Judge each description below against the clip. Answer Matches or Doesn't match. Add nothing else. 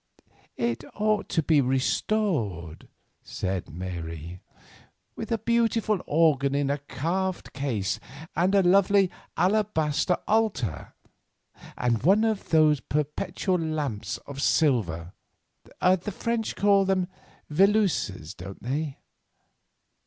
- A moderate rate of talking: Doesn't match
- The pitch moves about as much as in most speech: Doesn't match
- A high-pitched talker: Doesn't match